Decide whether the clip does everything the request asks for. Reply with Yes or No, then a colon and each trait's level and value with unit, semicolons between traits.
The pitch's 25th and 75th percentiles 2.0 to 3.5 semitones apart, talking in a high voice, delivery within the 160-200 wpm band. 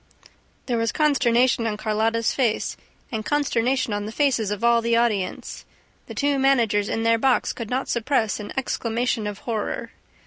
Yes: average, 2.8 semitones; high, 230 Hz; average, 165 wpm